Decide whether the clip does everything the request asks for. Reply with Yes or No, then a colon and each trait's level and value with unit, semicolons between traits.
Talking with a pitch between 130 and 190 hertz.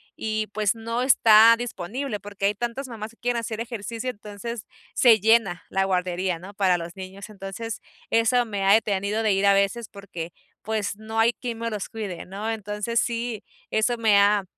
No: high, 215 Hz